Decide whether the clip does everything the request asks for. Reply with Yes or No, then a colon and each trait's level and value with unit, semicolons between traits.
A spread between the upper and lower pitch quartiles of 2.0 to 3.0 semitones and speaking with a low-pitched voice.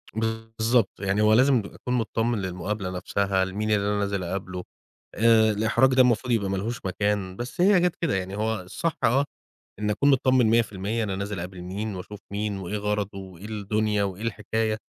Yes: narrow, 2.6 semitones; low, 105 Hz